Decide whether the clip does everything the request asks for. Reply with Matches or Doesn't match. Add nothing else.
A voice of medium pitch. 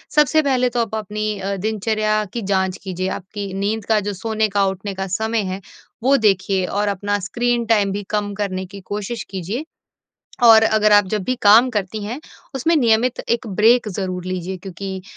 Doesn't match